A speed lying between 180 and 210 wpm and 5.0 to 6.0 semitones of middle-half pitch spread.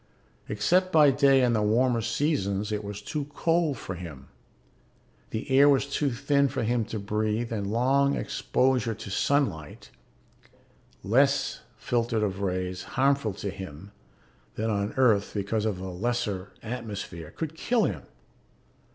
No: average, 145 wpm; wide, 5.4 semitones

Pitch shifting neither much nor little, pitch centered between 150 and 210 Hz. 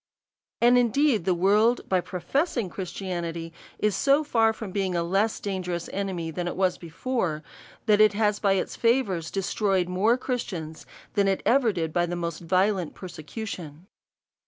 Yes: average, 4.1 semitones; high, 190 Hz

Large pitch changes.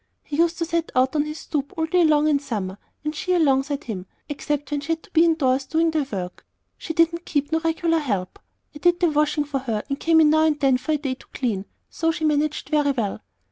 No: average, 3.1 semitones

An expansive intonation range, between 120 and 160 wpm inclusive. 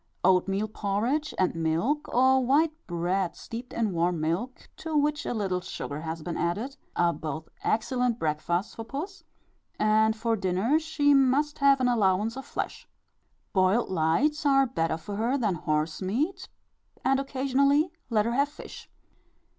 Yes: wide, 7.2 semitones; average, 155 wpm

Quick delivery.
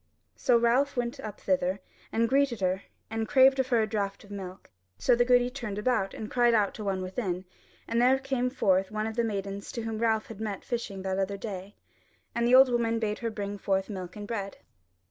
Yes: fast, 215 wpm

